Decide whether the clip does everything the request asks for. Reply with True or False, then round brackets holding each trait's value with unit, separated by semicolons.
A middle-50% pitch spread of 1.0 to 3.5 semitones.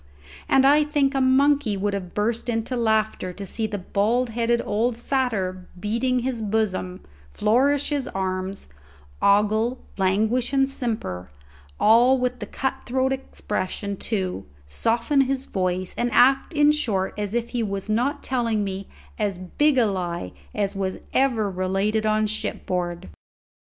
False (4.6 semitones)